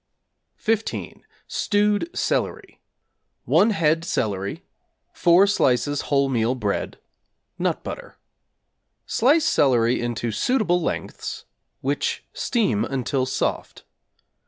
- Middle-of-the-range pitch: Yes, medium, 145 Hz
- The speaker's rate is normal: No, slow, 90 wpm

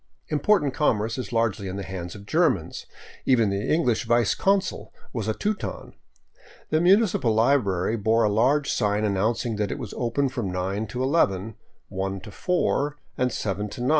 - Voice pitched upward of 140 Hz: No, low, 115 Hz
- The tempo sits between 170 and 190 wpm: Yes, average, 175 wpm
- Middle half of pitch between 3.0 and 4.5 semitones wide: No, wide, 5.6 semitones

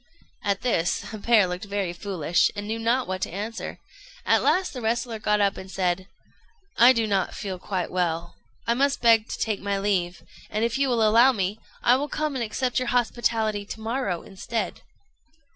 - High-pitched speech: Yes, high, 215 Hz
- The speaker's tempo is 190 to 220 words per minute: Yes, average, 195 wpm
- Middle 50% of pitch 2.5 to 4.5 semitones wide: Yes, average, 3.7 semitones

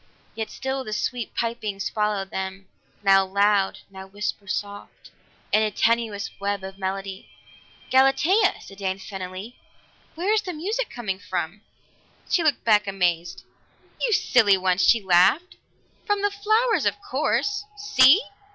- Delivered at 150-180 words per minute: No, average, 140 wpm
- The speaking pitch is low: No, high, 210 Hz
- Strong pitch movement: Yes, wide, 6.4 semitones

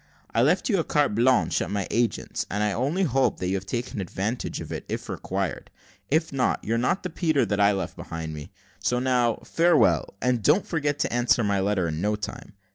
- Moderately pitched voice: No, low, 120 Hz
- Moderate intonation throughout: No, wide, 5.8 semitones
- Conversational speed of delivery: No, fast, 215 wpm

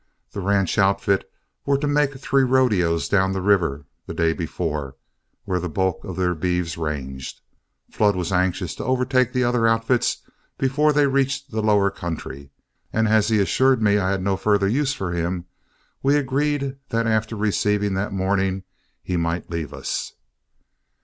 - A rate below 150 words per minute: No, average, 165 wpm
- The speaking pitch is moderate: No, low, 100 Hz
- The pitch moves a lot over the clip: Yes, wide, 6.1 semitones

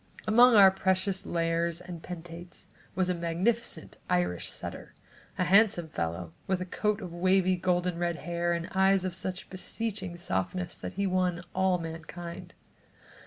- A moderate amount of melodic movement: No, narrow, 1.9 semitones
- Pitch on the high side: No, medium, 180 Hz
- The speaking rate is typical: Yes, average, 150 wpm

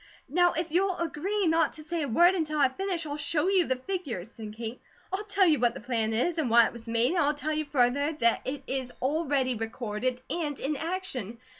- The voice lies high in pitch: Yes, very high, 290 Hz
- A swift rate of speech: Yes, fast, 230 wpm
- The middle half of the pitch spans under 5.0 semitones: No, wide, 5.6 semitones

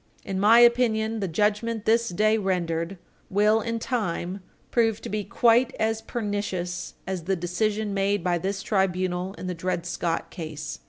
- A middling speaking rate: Yes, average, 160 wpm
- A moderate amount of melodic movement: Yes, average, 3.6 semitones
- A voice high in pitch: Yes, high, 200 Hz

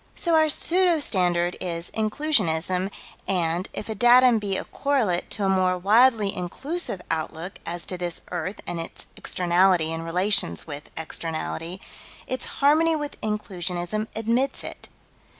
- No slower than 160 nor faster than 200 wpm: No, average, 140 wpm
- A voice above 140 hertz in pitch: Yes, high, 190 Hz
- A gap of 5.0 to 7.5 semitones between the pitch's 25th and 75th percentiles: Yes, wide, 5.6 semitones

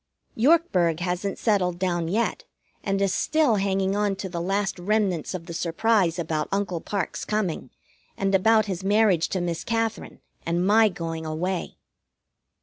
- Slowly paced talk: No, average, 150 wpm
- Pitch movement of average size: Yes, average, 3.2 semitones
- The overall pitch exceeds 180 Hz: Yes, high, 190 Hz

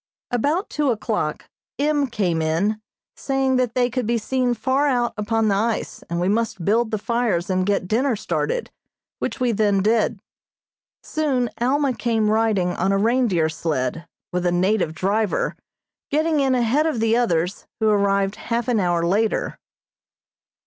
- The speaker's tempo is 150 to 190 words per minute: Yes, average, 160 wpm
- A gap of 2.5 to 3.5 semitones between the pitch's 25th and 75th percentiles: No, average, 4.3 semitones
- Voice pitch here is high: Yes, high, 220 Hz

